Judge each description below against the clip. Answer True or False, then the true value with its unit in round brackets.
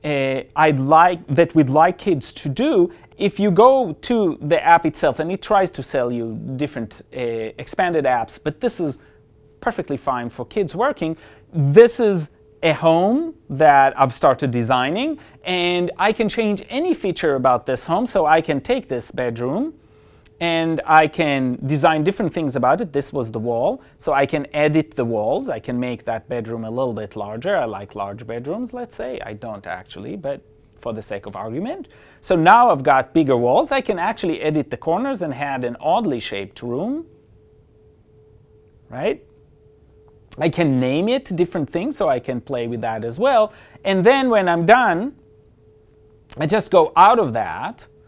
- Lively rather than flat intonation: True (7.0 semitones)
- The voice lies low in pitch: False (145 Hz)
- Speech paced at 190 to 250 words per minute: False (180 wpm)